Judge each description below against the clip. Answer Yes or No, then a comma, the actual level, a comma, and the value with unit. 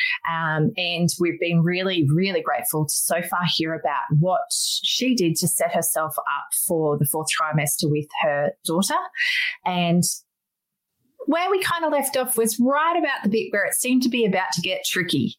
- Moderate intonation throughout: No, wide, 8.4 semitones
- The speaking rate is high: No, average, 185 wpm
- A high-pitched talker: No, medium, 180 Hz